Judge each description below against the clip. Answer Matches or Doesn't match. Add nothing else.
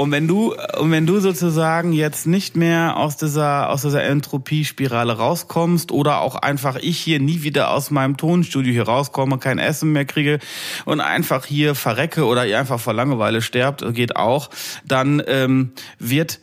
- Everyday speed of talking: Matches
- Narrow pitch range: Doesn't match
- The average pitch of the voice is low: Doesn't match